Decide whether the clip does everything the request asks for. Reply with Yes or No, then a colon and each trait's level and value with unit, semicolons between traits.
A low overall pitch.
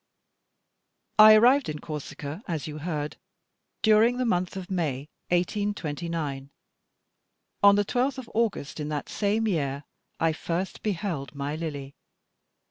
No: medium, 170 Hz